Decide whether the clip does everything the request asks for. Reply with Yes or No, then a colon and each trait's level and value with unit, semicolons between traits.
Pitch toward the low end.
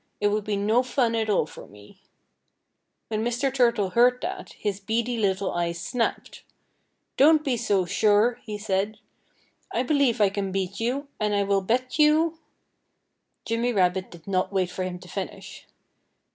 No: high, 215 Hz